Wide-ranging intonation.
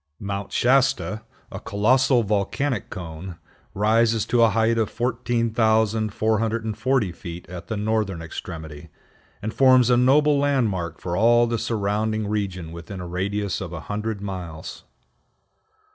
No: average, 3.7 semitones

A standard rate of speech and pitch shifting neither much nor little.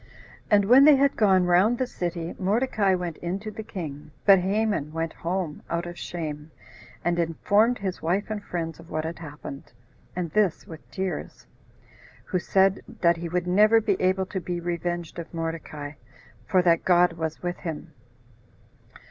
Yes: average, 170 wpm; average, 3.0 semitones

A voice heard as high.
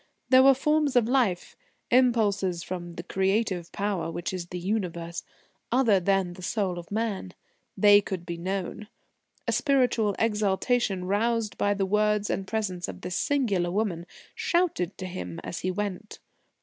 Yes: high, 200 Hz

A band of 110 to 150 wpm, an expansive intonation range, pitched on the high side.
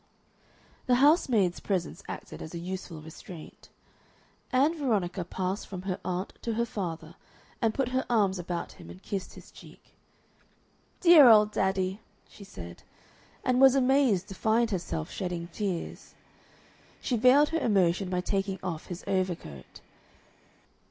No: average, 140 wpm; average, 5.0 semitones; high, 195 Hz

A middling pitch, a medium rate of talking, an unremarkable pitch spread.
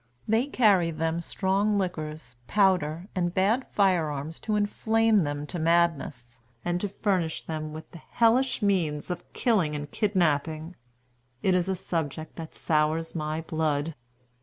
Yes: medium, 170 Hz; average, 145 wpm; average, 4.1 semitones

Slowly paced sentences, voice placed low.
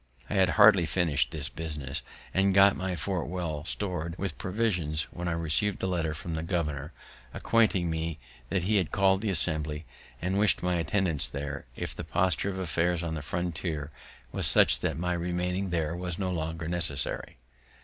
No: average, 180 wpm; very low, 85 Hz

